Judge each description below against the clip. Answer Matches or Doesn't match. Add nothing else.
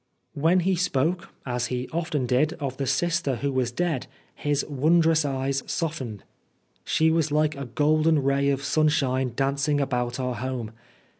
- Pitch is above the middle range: Doesn't match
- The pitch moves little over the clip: Doesn't match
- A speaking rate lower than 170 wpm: Matches